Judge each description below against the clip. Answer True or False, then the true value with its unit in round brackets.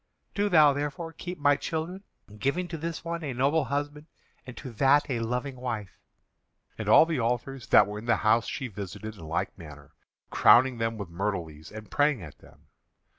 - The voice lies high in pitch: False (125 Hz)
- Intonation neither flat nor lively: False (5.9 semitones)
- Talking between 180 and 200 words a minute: True (190 wpm)